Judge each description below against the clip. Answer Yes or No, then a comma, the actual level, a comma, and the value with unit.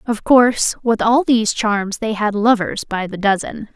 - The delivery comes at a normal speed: Yes, average, 190 wpm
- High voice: Yes, high, 220 Hz